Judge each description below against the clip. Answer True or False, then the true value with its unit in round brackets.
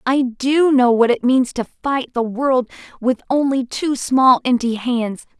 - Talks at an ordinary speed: True (180 wpm)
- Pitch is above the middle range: True (255 Hz)